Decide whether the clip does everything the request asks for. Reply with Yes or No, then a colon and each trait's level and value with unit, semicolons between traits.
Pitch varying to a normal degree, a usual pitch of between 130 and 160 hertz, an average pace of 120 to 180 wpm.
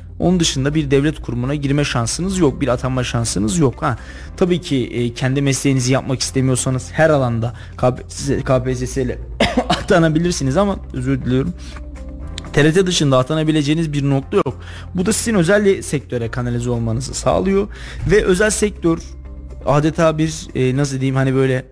Yes: average, 4.4 semitones; low, 135 Hz; fast, 140 wpm